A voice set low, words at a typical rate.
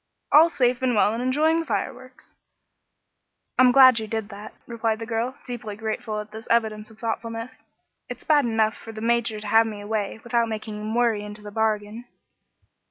No: high, 225 Hz; average, 185 wpm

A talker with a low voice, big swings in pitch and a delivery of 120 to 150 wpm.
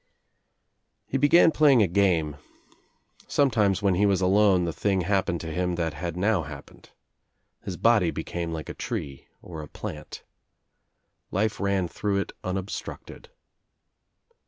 No: very low, 95 Hz; average, 3.4 semitones; average, 140 wpm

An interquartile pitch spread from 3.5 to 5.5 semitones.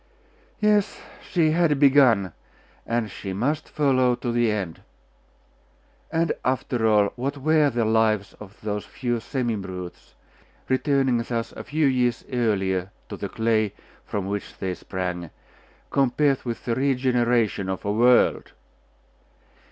Yes: average, 4.8 semitones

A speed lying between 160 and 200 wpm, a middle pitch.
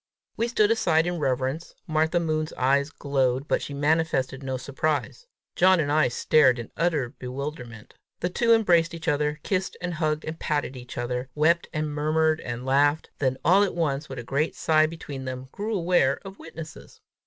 Yes: average, 180 wpm; medium, 150 Hz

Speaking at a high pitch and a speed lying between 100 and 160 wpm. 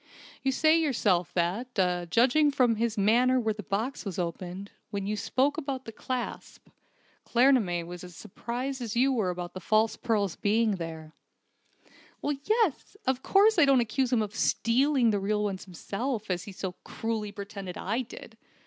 No: high, 220 Hz; average, 170 wpm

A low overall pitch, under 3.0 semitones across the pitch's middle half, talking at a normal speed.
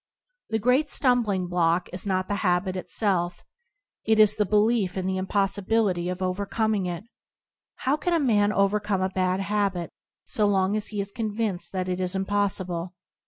No: high, 195 Hz; narrow, 2.4 semitones; average, 165 wpm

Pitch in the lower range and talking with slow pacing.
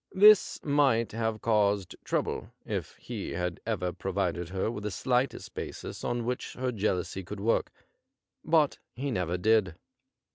No: low, 110 Hz; average, 145 wpm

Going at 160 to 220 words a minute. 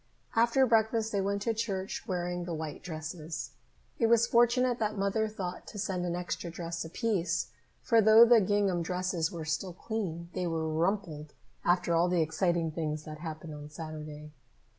Yes: average, 170 wpm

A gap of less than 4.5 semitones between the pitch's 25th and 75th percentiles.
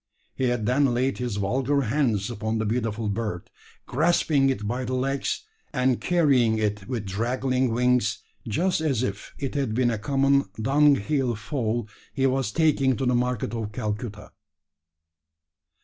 Yes: average, 3.6 semitones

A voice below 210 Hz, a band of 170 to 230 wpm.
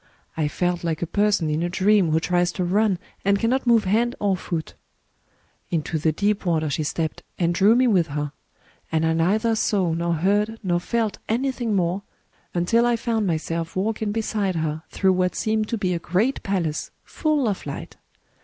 Yes: medium, 185 Hz; average, 185 wpm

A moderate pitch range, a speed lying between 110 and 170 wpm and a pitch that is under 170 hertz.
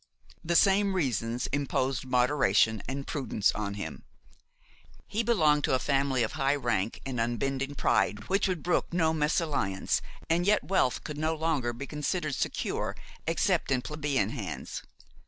Yes: average, 4.7 semitones; average, 150 wpm; medium, 140 Hz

